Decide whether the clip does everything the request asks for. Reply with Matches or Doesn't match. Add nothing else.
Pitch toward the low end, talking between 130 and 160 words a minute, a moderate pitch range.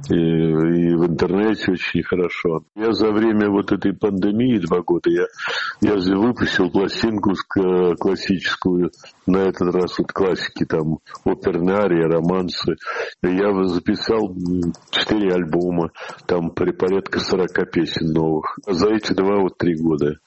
Matches